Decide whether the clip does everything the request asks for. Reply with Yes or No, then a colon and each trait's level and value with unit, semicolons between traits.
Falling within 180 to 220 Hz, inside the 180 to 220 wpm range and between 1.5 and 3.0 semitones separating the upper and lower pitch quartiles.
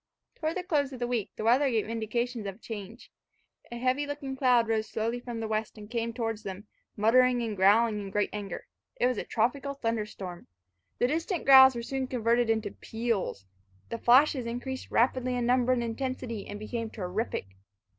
No: high, 235 Hz; average, 185 wpm; average, 2.7 semitones